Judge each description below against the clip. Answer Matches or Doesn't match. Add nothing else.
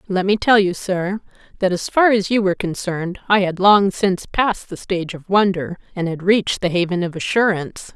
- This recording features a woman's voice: Matches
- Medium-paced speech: Doesn't match